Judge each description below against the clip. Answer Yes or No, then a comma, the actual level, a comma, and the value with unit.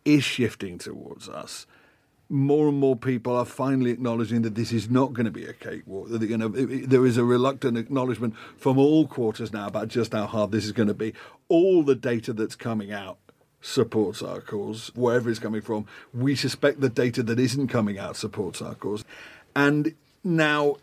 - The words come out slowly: No, average, 185 wpm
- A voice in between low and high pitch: No, low, 125 Hz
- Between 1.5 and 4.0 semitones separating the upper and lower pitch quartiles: Yes, average, 3.3 semitones